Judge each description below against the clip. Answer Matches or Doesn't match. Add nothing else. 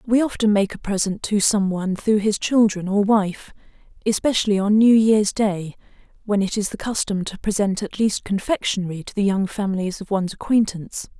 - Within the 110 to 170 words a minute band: Doesn't match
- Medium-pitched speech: Doesn't match